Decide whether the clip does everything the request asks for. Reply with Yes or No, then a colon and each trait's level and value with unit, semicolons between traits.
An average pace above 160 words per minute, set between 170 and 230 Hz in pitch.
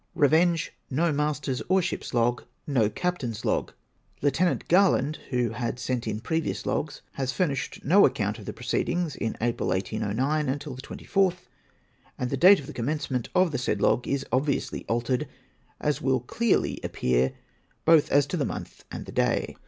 No: average, 170 wpm; low, 135 Hz